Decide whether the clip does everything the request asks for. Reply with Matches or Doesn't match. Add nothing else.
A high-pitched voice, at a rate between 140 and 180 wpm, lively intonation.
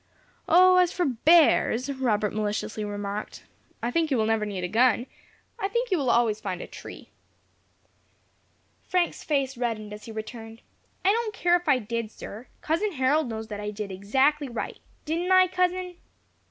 Matches